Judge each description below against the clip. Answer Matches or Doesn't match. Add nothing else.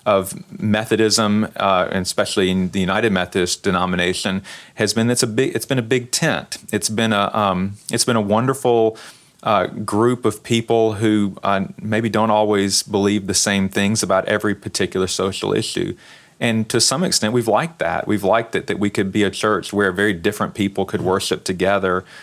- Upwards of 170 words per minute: Matches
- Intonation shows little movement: Matches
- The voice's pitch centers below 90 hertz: Doesn't match